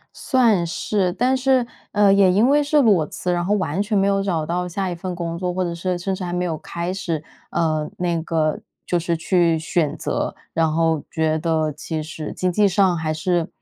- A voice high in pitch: No, medium, 175 Hz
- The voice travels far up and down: No, average, 3.2 semitones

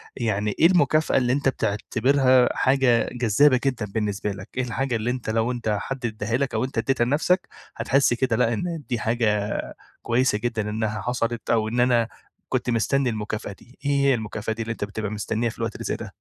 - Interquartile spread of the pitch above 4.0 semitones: No, average, 3.1 semitones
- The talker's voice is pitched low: Yes, low, 120 Hz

